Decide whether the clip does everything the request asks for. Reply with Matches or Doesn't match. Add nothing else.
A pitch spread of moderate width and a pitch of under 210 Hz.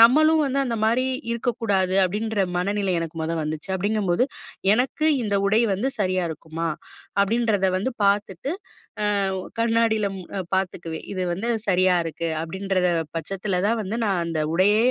Matches